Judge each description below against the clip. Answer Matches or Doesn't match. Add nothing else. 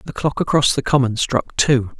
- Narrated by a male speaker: Matches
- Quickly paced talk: Matches